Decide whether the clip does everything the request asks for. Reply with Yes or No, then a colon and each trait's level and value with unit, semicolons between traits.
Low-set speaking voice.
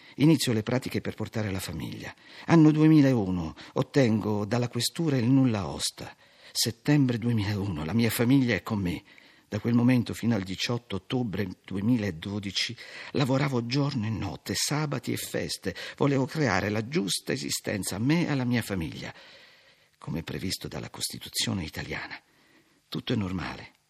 Yes: low, 120 Hz